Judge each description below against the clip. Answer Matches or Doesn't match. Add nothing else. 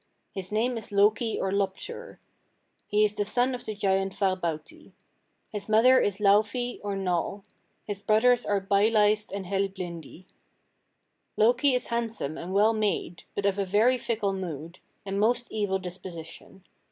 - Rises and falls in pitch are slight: Matches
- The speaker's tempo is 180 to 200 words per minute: Doesn't match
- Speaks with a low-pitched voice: Doesn't match